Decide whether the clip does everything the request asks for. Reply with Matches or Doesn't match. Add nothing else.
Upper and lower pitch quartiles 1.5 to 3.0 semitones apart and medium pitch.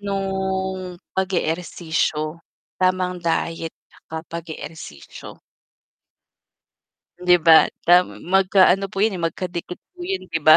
Matches